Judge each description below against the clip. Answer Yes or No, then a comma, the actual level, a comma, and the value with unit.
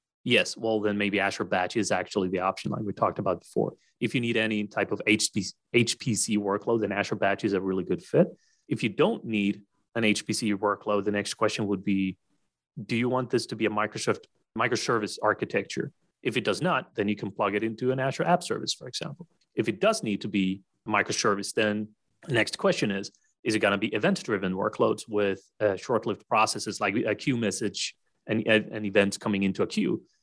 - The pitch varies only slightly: Yes, narrow, 1.7 semitones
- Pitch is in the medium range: No, low, 105 Hz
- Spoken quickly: Yes, fast, 210 wpm